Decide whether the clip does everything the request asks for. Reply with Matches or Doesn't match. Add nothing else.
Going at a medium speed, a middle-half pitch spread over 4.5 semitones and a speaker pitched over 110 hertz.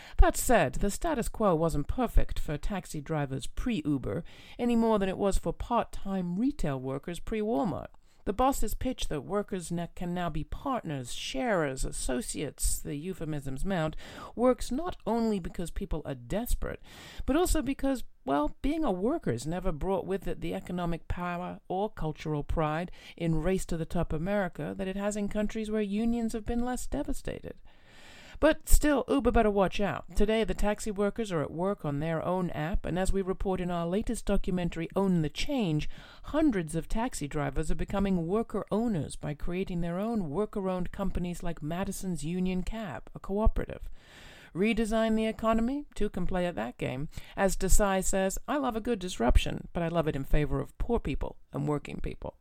Matches